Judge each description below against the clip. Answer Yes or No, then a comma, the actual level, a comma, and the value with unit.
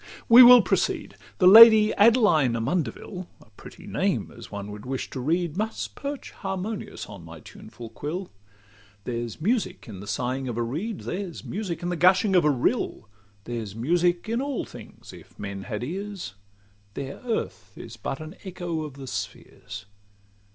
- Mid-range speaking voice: Yes, medium, 155 Hz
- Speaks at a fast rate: No, average, 165 wpm